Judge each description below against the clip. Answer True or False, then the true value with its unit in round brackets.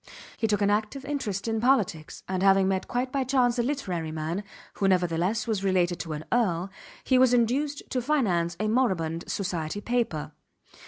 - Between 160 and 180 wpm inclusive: True (175 wpm)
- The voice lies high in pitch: True (205 Hz)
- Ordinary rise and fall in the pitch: False (5.8 semitones)